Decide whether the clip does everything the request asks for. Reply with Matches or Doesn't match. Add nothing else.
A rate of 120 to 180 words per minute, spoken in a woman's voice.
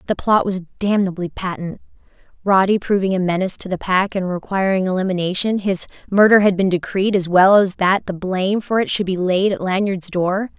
Doesn't match